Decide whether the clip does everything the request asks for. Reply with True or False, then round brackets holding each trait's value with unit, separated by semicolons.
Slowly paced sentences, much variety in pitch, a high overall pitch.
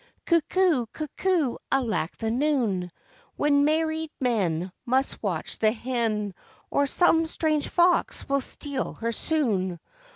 True (120 wpm; 6.2 semitones; 265 Hz)